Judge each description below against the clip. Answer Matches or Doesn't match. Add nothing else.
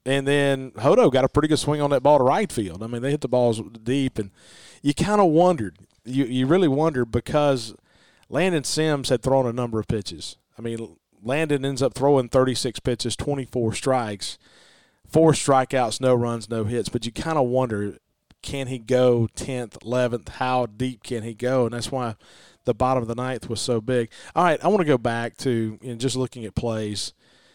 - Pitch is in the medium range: Doesn't match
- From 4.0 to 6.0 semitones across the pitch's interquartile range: Doesn't match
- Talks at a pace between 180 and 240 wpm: Matches